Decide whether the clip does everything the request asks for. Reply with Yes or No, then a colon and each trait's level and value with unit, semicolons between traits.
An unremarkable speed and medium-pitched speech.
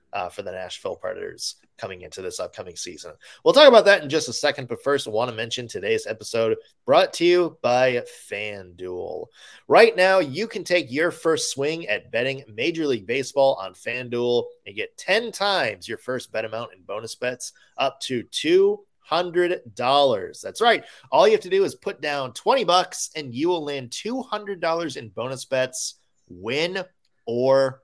Yes: average, 175 wpm; medium, 165 Hz